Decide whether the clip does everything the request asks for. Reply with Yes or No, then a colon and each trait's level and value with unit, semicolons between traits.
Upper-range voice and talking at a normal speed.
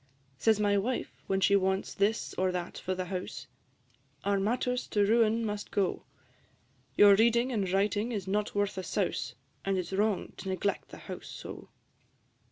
Yes: high, 200 Hz; average, 175 wpm